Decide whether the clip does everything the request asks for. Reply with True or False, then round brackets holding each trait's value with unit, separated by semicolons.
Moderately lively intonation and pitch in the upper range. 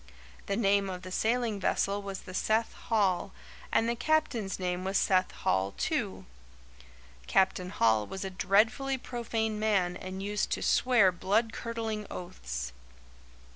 True (3.4 semitones; 200 Hz)